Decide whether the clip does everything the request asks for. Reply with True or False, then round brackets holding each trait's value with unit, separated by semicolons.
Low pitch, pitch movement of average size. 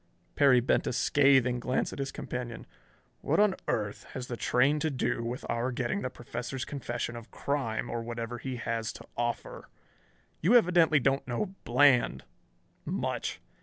True (125 Hz; 3.0 semitones)